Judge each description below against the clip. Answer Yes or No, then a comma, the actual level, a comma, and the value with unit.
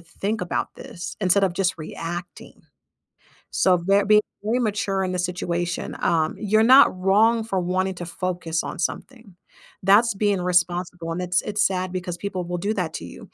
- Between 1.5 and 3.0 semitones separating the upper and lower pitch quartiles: Yes, average, 2.7 semitones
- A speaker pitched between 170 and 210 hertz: Yes, medium, 185 Hz